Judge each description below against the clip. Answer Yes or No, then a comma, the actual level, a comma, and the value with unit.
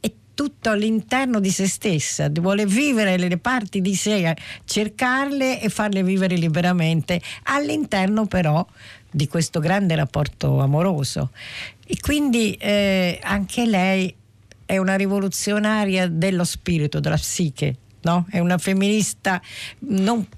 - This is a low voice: No, high, 190 Hz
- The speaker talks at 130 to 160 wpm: No, average, 120 wpm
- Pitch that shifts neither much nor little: Yes, average, 4.3 semitones